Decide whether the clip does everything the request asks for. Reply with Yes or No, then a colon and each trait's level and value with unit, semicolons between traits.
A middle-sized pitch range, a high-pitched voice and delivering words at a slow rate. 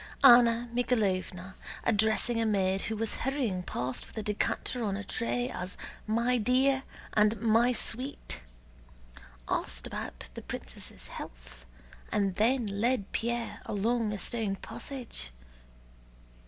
Yes: average, 3.7 semitones; high, 220 Hz; slow, 125 wpm